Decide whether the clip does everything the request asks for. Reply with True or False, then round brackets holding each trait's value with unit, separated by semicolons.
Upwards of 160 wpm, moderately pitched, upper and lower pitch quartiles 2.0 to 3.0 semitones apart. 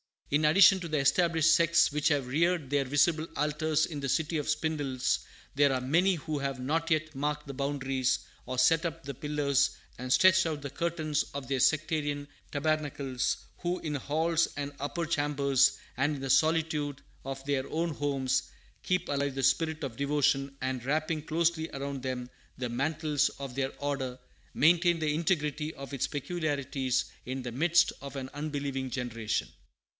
True (170 wpm; 145 Hz; 2.7 semitones)